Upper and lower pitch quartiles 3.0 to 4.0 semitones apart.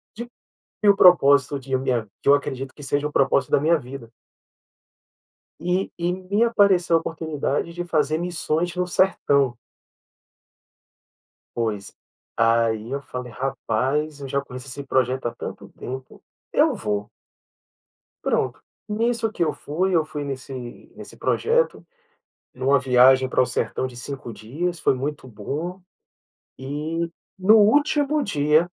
No: average, 5.2 semitones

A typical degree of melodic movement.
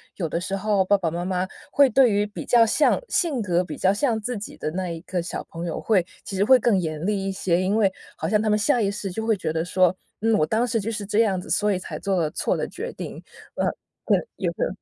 Yes: average, 3.4 semitones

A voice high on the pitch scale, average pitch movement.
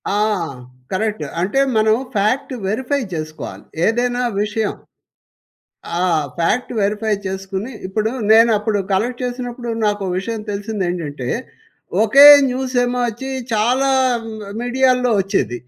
Yes: high, 220 Hz; average, 3.7 semitones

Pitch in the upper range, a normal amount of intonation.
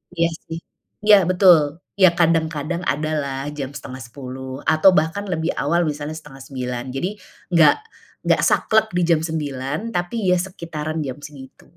No: medium, 155 Hz; average, 4.0 semitones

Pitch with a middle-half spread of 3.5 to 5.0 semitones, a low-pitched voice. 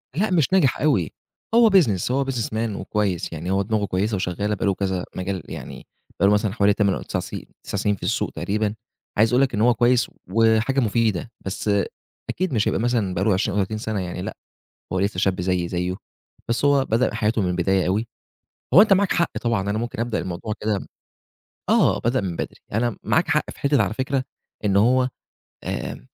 Yes: average, 4.1 semitones; low, 105 Hz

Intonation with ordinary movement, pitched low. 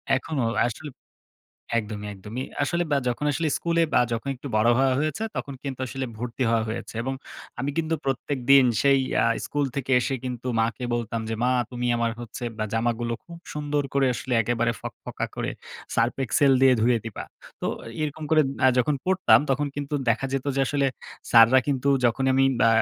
Yes: average, 3.3 semitones; low, 130 Hz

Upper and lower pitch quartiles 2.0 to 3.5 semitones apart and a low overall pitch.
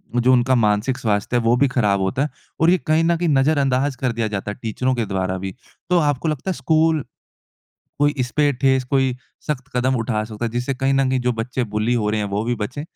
No: average, 4.2 semitones; low, 125 Hz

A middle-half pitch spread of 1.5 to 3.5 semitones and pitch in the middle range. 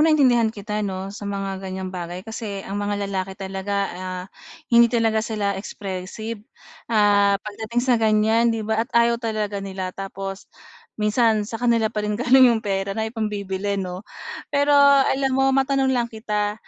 No: average, 2.8 semitones; high, 210 Hz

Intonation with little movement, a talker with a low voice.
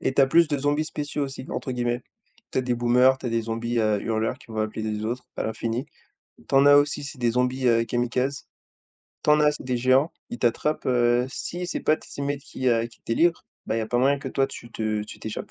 No: average, 3.4 semitones; low, 125 Hz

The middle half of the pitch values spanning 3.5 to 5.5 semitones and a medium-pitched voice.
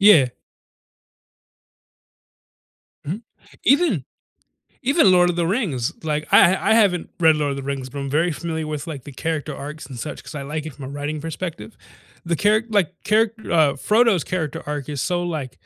Yes: average, 4.3 semitones; medium, 160 Hz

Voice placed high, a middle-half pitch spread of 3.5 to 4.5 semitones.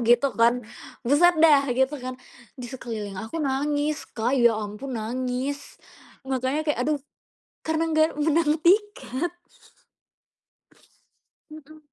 Yes: very high, 275 Hz; average, 4.2 semitones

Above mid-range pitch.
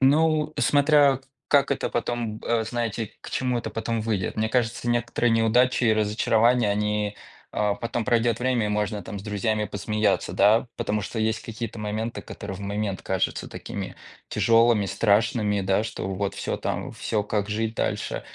No: low, 110 Hz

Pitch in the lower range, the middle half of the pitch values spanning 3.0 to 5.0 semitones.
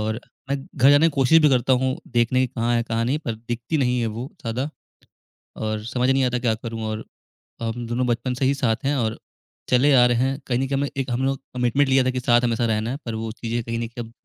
No: low, 125 Hz; narrow, 2.5 semitones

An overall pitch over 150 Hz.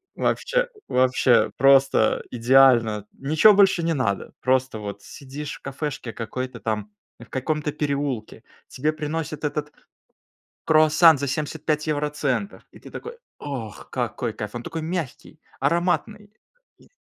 No: medium, 140 Hz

